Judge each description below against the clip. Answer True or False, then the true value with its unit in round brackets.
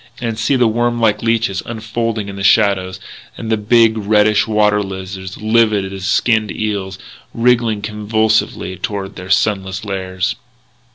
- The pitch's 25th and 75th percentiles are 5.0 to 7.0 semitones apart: False (2.6 semitones)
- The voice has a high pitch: False (105 Hz)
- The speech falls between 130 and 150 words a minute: True (145 wpm)